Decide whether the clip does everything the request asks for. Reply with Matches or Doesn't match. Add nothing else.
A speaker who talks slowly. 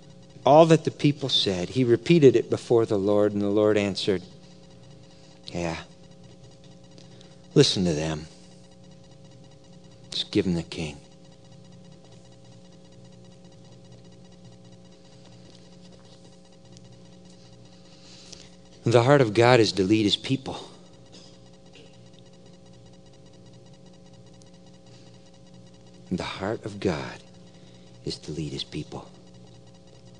Matches